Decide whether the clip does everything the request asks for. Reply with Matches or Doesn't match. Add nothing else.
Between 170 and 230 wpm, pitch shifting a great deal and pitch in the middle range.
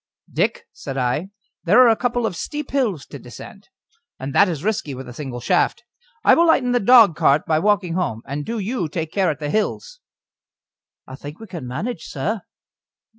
Matches